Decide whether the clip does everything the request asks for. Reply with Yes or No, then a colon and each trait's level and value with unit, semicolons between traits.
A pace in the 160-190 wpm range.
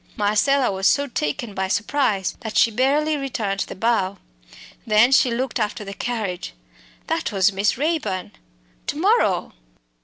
No: average, 145 wpm